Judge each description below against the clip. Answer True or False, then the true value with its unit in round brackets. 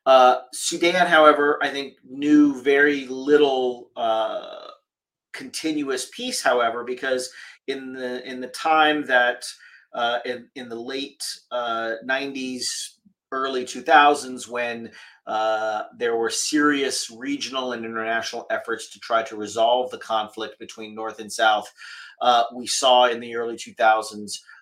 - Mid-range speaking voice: False (125 Hz)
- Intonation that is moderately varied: True (3.9 semitones)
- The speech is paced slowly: True (130 wpm)